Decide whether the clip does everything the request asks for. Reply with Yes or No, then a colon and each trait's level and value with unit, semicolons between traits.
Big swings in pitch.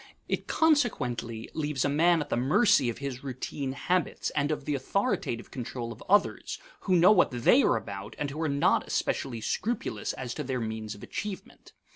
Yes: wide, 6.5 semitones